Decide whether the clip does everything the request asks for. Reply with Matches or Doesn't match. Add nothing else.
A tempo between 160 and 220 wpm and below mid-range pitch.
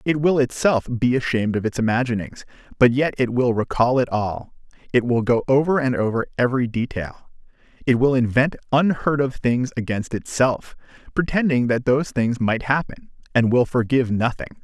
Matches